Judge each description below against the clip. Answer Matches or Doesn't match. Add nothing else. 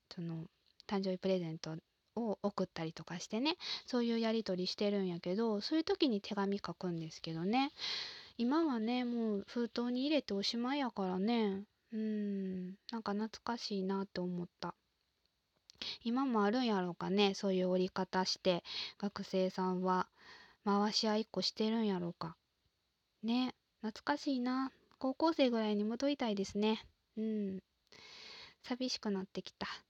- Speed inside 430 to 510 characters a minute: Doesn't match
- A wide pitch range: Doesn't match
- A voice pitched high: Matches